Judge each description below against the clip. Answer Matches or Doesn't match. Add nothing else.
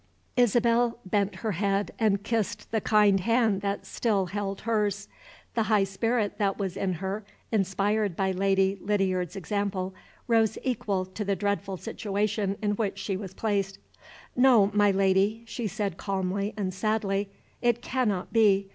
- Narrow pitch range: Matches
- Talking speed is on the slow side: Doesn't match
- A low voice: Doesn't match